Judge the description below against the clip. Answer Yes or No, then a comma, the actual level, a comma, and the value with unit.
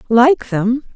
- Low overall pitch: No, high, 245 Hz